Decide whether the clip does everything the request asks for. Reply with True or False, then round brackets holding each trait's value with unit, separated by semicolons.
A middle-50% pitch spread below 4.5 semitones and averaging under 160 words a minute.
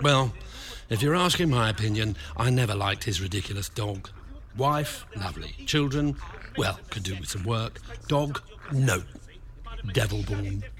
False (4.9 semitones; 140 wpm)